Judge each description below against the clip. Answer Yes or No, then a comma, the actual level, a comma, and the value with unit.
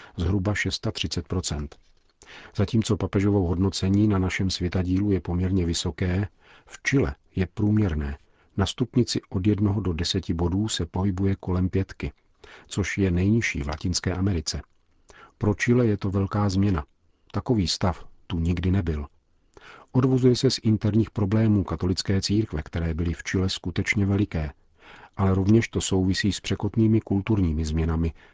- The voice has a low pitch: Yes, very low, 95 Hz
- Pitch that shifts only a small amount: No, average, 3.1 semitones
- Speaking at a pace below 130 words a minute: No, average, 135 wpm